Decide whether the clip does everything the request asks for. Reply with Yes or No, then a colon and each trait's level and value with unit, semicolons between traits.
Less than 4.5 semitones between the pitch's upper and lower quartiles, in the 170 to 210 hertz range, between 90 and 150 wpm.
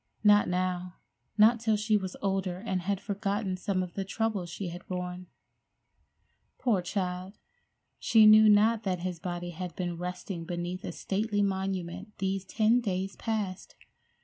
Yes: narrow, 2.6 semitones; high, 190 Hz; average, 145 wpm